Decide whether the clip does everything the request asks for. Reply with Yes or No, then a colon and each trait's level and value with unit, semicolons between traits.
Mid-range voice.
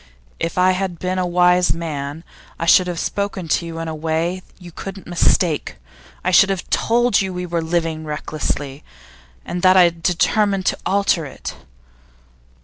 Yes: medium, 175 Hz